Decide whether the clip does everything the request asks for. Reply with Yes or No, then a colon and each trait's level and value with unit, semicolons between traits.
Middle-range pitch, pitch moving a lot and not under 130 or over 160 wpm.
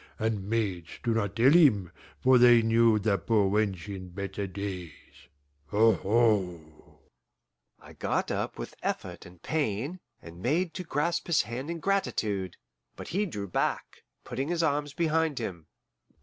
No: low, 110 Hz; wide, 6.9 semitones; average, 150 wpm